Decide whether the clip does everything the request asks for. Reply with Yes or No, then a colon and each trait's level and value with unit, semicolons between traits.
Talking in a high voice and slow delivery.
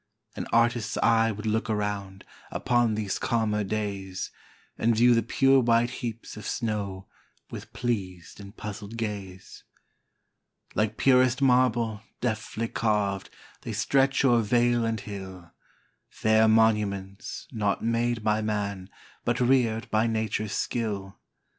No: low, 110 Hz; slow, 125 wpm